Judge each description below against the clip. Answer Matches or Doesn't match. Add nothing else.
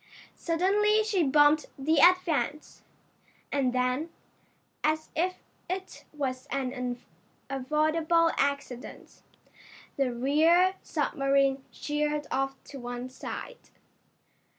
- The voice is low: Doesn't match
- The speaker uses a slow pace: Matches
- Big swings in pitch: Doesn't match